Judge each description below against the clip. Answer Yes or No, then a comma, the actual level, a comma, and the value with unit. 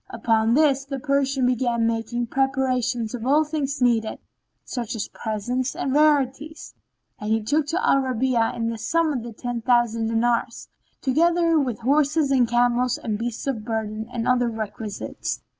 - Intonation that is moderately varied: Yes, average, 3.2 semitones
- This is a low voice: No, high, 245 Hz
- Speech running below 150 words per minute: No, average, 160 wpm